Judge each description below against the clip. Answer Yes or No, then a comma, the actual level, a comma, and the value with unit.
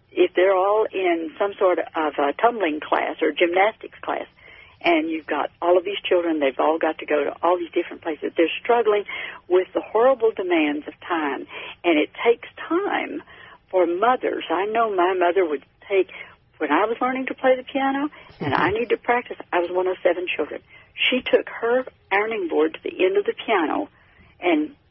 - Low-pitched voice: No, high, 225 Hz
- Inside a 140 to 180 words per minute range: No, average, 195 wpm